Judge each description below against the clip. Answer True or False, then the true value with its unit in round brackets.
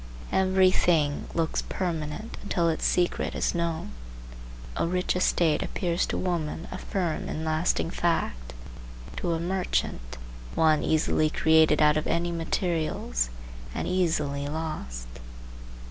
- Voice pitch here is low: False (165 Hz)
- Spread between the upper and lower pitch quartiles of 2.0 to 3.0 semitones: True (2.5 semitones)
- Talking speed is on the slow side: True (125 wpm)